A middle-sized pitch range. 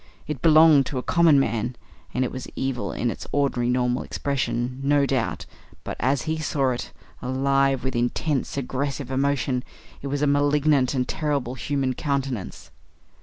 No: narrow, 2.2 semitones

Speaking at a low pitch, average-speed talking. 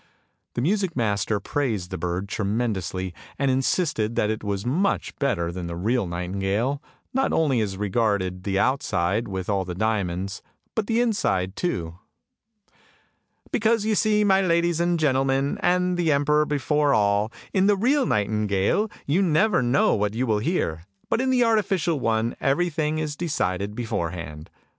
Yes: low, 120 Hz; average, 155 wpm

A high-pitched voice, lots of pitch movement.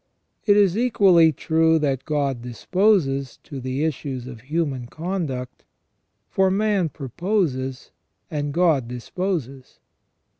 No: medium, 150 Hz; wide, 5.7 semitones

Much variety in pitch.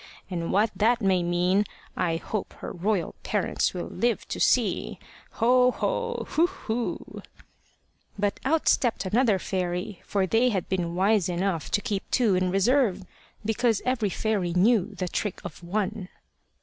No: average, 3.9 semitones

